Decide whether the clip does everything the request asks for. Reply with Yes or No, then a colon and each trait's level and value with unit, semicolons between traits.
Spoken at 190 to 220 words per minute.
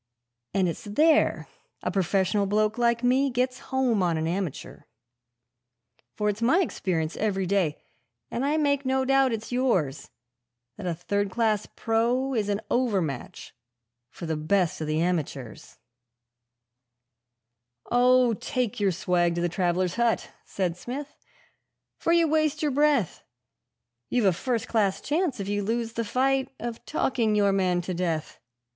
No: average, 150 wpm